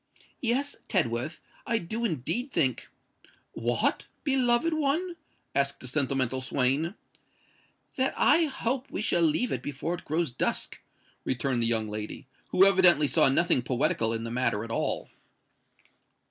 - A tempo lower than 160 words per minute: Yes, slow, 135 wpm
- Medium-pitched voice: Yes, medium, 155 Hz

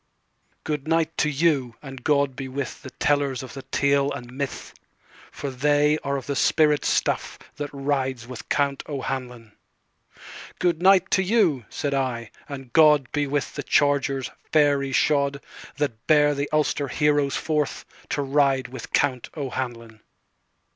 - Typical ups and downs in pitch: No, narrow, 2.0 semitones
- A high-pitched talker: No, medium, 140 Hz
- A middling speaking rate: No, slow, 130 wpm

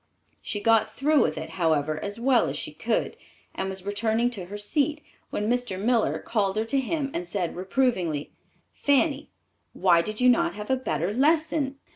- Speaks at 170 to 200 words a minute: Yes, average, 180 wpm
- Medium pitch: No, high, 220 Hz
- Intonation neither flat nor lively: No, wide, 5.8 semitones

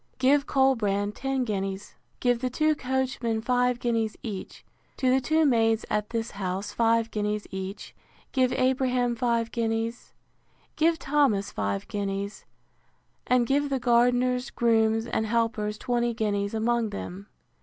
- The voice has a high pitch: Yes, high, 235 Hz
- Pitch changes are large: No, average, 3.2 semitones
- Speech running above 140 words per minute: No, slow, 135 wpm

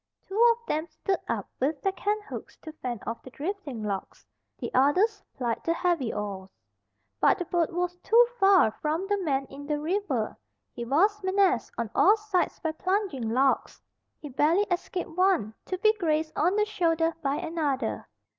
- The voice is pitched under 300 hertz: No, very high, 330 Hz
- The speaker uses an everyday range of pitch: No, wide, 6.2 semitones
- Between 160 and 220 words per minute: Yes, average, 175 wpm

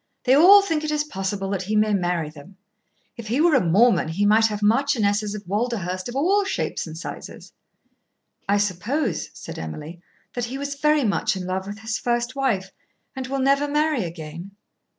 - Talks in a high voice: Yes, high, 215 Hz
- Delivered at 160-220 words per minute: Yes, average, 190 wpm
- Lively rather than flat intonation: Yes, wide, 6.4 semitones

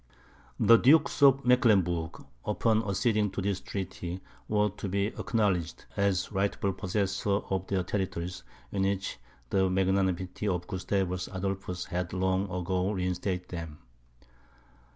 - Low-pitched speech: Yes, very low, 95 Hz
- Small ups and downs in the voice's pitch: Yes, narrow, 1.9 semitones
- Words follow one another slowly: Yes, slow, 125 wpm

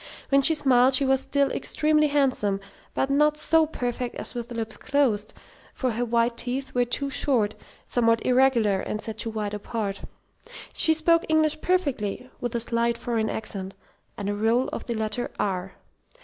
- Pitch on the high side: Yes, high, 245 Hz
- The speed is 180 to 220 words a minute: No, average, 170 wpm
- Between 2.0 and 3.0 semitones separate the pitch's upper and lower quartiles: No, average, 4.0 semitones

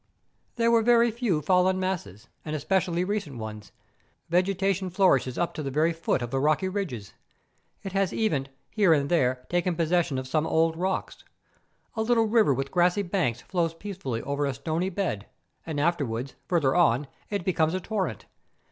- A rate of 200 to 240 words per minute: No, average, 170 wpm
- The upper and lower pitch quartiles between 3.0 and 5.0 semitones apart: No, wide, 5.4 semitones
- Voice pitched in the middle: Yes, medium, 170 Hz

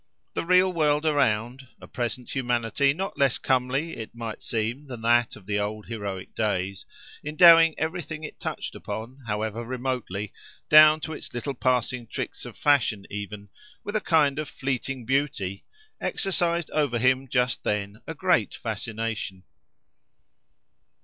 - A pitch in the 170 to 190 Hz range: No, low, 125 Hz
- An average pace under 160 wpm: Yes, slow, 135 wpm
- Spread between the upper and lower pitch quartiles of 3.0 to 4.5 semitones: No, average, 5.3 semitones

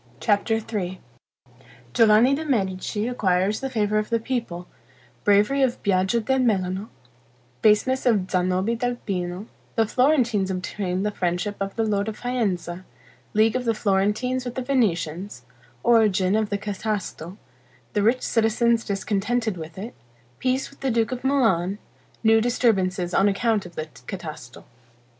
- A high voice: Yes, high, 210 Hz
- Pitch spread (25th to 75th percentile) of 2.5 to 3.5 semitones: No, average, 3.9 semitones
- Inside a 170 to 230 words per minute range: No, average, 145 wpm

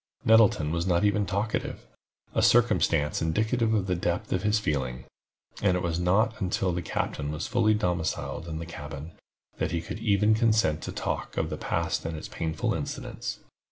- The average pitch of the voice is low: Yes, very low, 90 Hz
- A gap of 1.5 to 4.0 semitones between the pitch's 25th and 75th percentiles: No, average, 4.9 semitones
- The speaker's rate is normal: Yes, average, 165 wpm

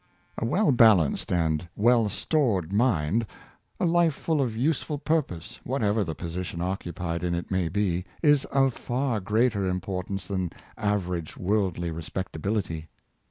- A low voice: Yes, low, 100 Hz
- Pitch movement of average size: No, wide, 5.7 semitones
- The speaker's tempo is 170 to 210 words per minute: No, average, 140 wpm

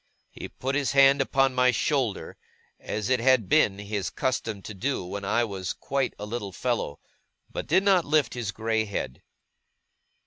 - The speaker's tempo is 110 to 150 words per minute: No, average, 170 wpm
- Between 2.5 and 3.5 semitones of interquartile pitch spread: No, average, 4.8 semitones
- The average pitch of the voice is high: No, low, 120 Hz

